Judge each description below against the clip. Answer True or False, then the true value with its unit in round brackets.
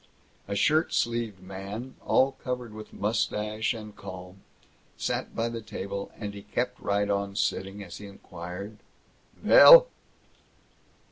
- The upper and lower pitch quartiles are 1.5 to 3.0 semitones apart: True (2.7 semitones)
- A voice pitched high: False (105 Hz)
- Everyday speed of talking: False (130 wpm)